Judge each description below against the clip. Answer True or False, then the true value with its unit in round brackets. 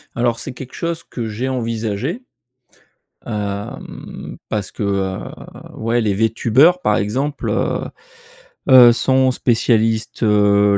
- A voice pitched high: False (115 Hz)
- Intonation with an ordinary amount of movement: True (3.7 semitones)